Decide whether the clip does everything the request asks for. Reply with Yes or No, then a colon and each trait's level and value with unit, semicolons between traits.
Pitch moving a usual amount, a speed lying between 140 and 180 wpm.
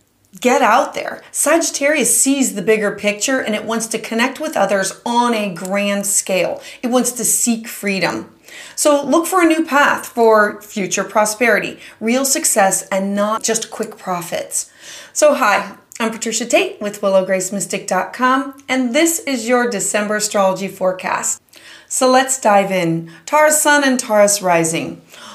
Yes: average, 4.7 semitones; average, 150 wpm